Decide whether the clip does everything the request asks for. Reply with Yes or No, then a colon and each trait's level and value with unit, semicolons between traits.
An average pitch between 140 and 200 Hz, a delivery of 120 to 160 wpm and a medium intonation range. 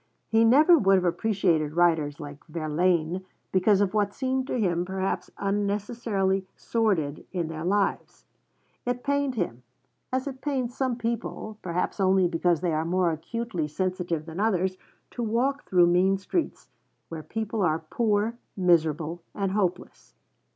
Yes: high, 190 Hz; average, 145 wpm; average, 4.8 semitones